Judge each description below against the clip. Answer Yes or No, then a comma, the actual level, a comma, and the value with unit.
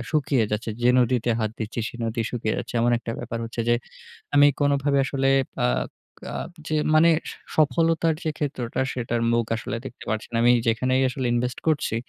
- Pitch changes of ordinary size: Yes, average, 3.6 semitones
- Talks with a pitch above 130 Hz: No, low, 125 Hz